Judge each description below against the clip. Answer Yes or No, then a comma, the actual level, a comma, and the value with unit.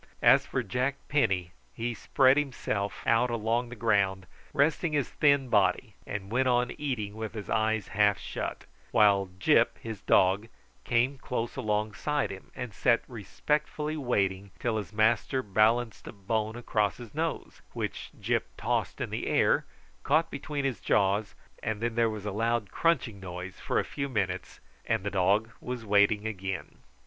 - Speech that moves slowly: No, average, 160 wpm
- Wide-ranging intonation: No, average, 3.7 semitones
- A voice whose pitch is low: Yes, low, 110 Hz